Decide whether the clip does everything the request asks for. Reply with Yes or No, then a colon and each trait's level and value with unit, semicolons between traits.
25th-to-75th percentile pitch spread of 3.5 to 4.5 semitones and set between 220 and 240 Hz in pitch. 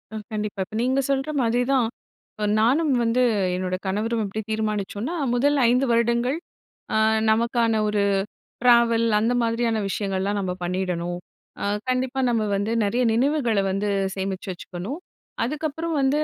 Yes: average, 3.8 semitones; high, 230 Hz